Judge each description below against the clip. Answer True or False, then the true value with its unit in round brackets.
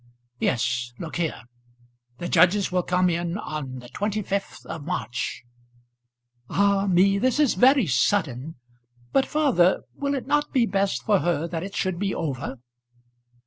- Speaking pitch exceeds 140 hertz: True (185 Hz)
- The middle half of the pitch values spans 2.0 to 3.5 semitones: False (4.1 semitones)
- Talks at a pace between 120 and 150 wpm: True (145 wpm)